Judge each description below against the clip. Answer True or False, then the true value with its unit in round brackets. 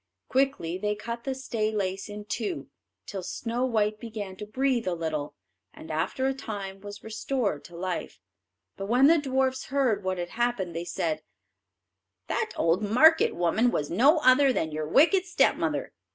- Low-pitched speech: False (215 Hz)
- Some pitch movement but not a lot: False (5.7 semitones)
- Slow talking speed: False (165 wpm)